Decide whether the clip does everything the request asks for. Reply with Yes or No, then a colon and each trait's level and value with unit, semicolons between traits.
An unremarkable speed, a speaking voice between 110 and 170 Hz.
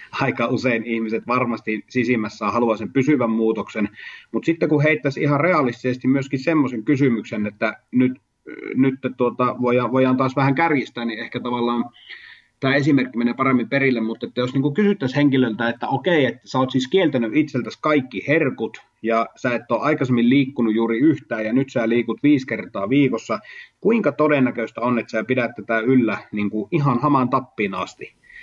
No: fast, 165 wpm; low, 125 Hz